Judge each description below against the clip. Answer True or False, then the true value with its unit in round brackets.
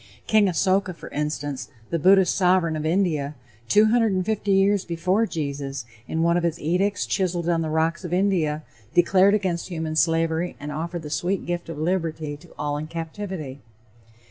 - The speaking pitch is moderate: True (170 Hz)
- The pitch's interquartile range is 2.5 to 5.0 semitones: True (3.2 semitones)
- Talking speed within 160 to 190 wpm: True (165 wpm)